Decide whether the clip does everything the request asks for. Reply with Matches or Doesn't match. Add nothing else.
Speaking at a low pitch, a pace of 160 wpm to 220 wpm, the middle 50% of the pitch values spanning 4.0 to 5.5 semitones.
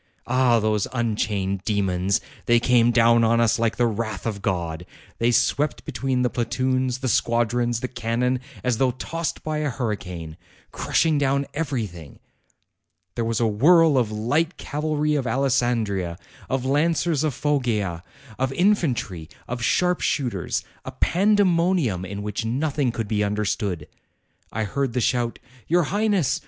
Doesn't match